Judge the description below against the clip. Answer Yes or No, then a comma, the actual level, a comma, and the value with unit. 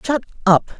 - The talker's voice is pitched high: Yes, high, 225 Hz